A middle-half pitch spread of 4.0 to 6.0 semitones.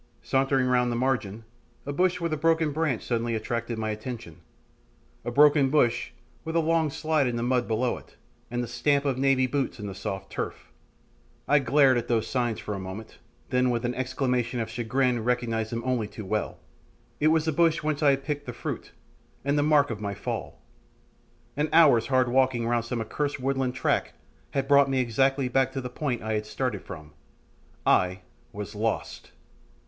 No: average, 3.5 semitones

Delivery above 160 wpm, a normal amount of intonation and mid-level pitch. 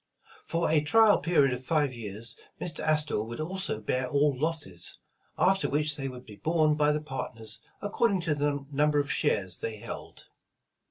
Yes: average, 170 wpm; average, 4.0 semitones; medium, 145 Hz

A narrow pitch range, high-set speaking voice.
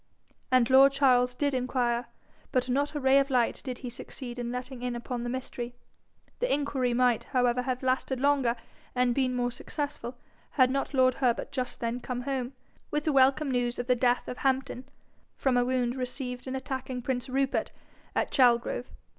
Yes: narrow, 1.5 semitones; very high, 255 Hz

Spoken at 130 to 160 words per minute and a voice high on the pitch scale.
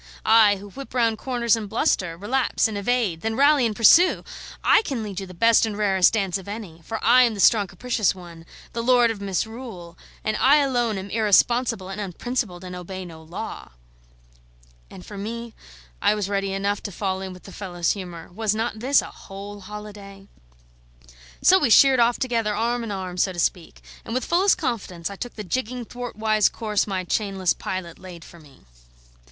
No: average, 190 wpm; high, 210 Hz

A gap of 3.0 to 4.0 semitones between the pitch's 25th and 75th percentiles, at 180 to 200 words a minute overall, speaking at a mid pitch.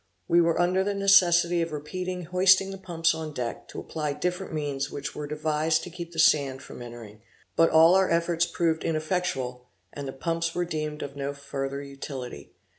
Yes: average, 3.6 semitones; average, 190 wpm; medium, 160 Hz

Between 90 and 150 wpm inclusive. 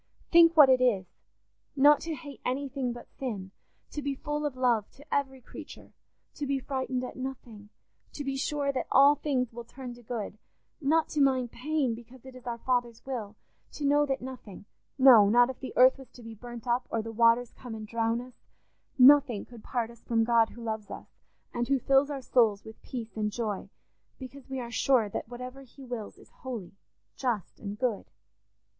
No: average, 190 wpm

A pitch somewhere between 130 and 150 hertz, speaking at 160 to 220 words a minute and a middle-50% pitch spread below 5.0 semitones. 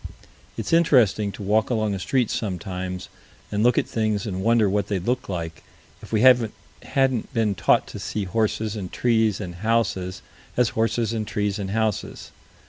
No: low, 105 Hz; average, 170 wpm; average, 2.9 semitones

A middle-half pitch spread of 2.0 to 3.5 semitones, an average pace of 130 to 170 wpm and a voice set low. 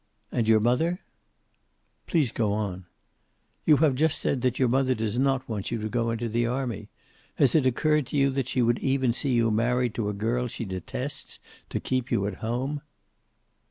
No: average, 3.1 semitones; average, 190 wpm; low, 120 Hz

